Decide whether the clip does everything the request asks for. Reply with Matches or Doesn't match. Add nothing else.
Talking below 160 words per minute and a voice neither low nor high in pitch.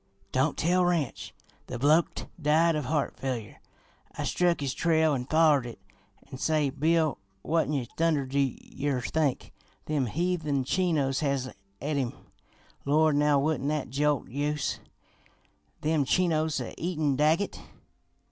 Matches